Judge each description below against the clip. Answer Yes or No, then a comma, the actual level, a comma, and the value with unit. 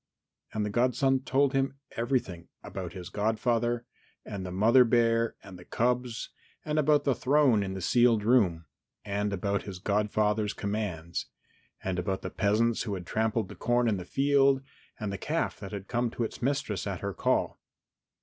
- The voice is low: Yes, low, 110 Hz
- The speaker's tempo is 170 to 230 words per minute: Yes, average, 175 wpm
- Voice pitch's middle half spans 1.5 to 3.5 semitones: No, average, 3.9 semitones